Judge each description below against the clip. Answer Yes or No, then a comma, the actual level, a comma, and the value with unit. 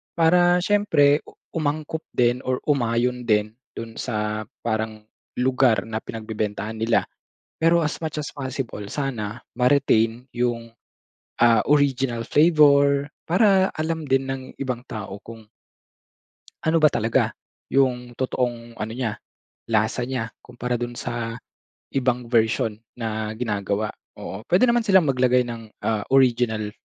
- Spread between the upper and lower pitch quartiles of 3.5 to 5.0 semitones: Yes, average, 4.0 semitones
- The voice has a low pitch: Yes, low, 125 Hz